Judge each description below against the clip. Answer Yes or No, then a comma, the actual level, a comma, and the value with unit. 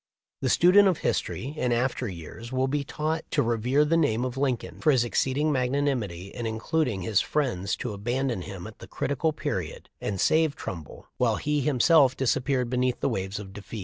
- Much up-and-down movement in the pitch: No, average, 4.6 semitones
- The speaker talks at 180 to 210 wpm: Yes, average, 185 wpm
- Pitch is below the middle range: Yes, low, 125 Hz